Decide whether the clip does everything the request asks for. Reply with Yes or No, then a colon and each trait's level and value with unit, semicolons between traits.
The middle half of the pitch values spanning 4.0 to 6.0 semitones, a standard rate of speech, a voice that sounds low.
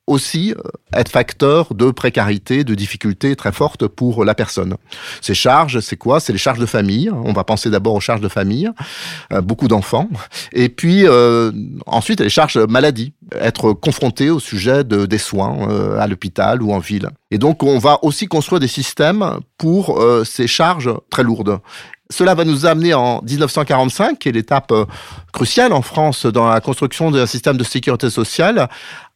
Yes: wide, 5.5 semitones; average, 175 wpm; low, 125 Hz